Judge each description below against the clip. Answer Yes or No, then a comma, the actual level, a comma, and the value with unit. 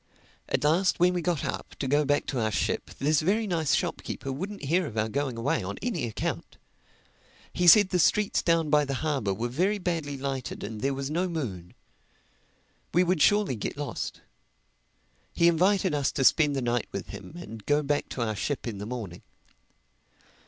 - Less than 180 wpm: No, average, 190 wpm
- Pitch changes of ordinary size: No, wide, 5.8 semitones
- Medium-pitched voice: Yes, medium, 145 Hz